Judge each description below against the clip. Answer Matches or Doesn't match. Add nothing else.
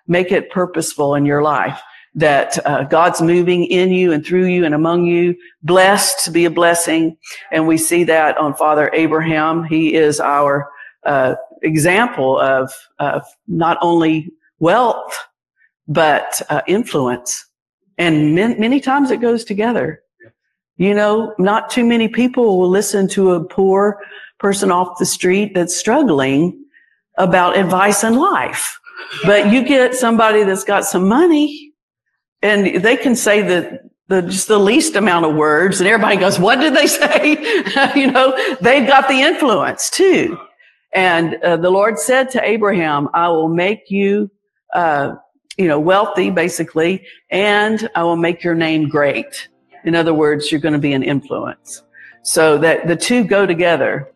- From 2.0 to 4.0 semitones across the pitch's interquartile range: Doesn't match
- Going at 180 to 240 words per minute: Doesn't match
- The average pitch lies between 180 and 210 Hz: Matches